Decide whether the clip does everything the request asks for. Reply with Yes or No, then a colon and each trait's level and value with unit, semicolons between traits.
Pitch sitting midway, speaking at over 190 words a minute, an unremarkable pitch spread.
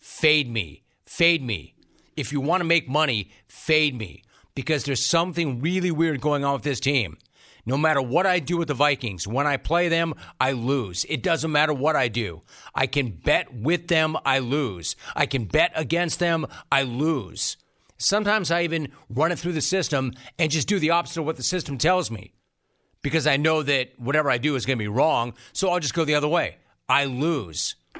Yes: medium, 145 Hz; fast, 205 wpm; average, 4.7 semitones